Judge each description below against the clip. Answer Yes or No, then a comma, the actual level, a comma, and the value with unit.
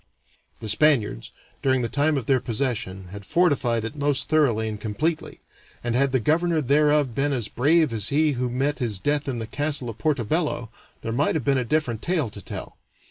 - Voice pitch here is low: Yes, low, 130 Hz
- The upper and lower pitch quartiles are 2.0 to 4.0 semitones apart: No, average, 4.6 semitones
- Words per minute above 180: Yes, average, 200 wpm